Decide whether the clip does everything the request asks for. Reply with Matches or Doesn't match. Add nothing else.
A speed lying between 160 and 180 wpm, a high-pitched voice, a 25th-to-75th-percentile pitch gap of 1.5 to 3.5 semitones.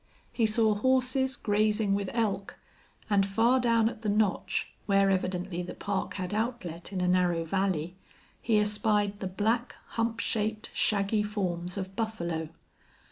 Doesn't match